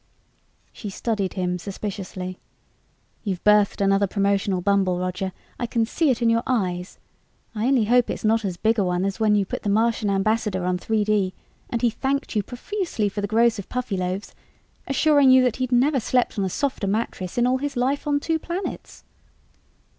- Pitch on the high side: Yes, high, 215 Hz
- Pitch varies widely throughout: No, average, 4.2 semitones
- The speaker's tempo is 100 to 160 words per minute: No, average, 185 wpm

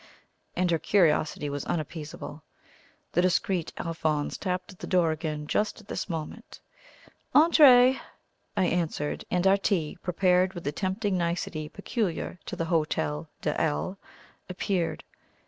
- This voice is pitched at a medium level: Yes, medium, 175 Hz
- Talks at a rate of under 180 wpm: Yes, slow, 135 wpm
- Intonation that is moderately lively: Yes, average, 3.5 semitones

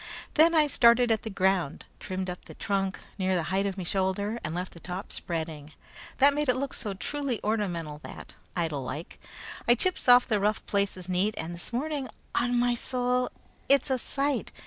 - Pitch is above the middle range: Yes, high, 205 Hz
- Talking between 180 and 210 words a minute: Yes, average, 190 wpm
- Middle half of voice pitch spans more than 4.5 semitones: Yes, wide, 5.6 semitones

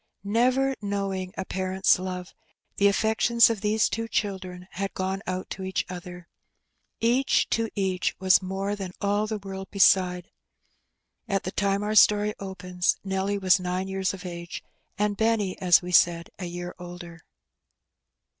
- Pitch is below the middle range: No, high, 190 Hz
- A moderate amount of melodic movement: No, narrow, 2.1 semitones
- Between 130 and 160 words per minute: Yes, average, 155 wpm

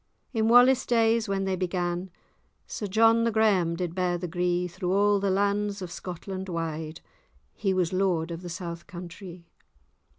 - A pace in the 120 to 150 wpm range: No, average, 165 wpm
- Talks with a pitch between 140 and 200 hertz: Yes, medium, 185 Hz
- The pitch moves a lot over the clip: No, average, 2.7 semitones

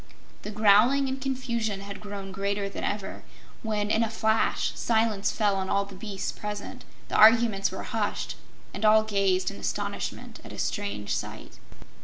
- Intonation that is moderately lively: No, narrow, 2.0 semitones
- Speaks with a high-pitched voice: Yes, high, 210 Hz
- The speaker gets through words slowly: No, average, 165 wpm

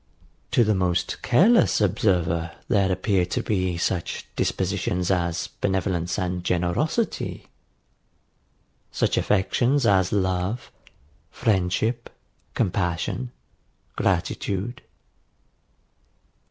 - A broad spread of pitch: No, average, 3.4 semitones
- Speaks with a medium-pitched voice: No, very low, 95 Hz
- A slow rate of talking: Yes, slow, 80 wpm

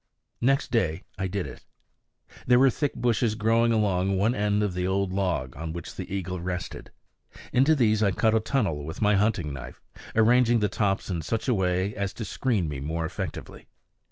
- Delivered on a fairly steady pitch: No, average, 4.0 semitones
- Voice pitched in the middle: No, low, 100 Hz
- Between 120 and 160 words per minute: No, average, 190 wpm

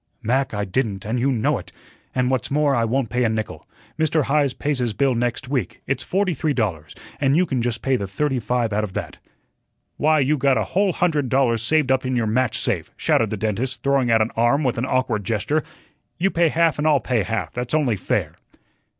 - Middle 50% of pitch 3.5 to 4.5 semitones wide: Yes, average, 4.1 semitones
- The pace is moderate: No, fast, 225 wpm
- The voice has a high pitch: No, low, 125 Hz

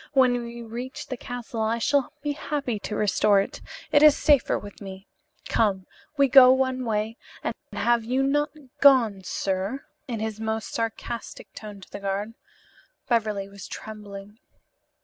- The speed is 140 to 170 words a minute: Yes, average, 155 wpm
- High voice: Yes, high, 225 Hz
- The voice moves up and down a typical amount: Yes, average, 3.8 semitones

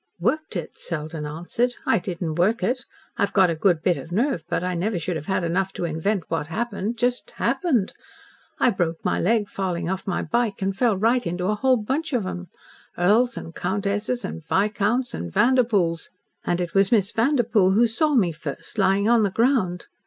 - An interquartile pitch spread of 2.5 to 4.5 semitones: No, average, 5.2 semitones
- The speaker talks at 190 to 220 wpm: Yes, average, 195 wpm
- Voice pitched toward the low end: No, high, 195 Hz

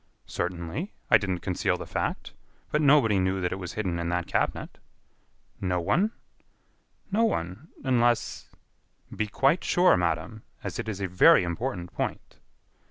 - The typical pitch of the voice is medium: No, very low, 95 Hz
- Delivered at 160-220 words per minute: No, average, 150 wpm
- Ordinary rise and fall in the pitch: No, wide, 7.0 semitones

